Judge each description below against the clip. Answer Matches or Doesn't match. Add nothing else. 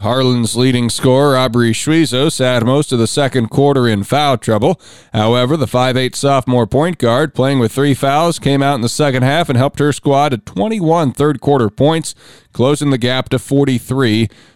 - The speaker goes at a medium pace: Matches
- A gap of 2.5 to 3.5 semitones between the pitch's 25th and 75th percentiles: Matches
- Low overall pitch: Matches